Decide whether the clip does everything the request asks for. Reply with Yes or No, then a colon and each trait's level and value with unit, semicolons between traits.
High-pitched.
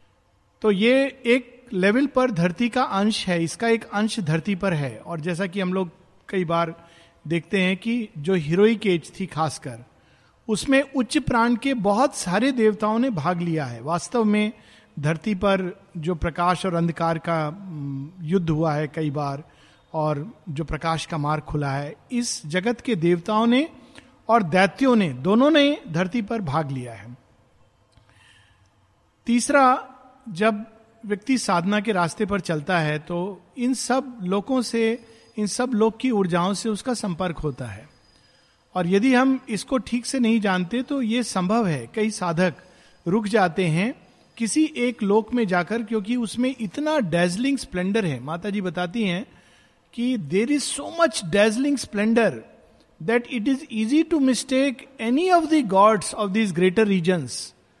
Yes: high, 205 Hz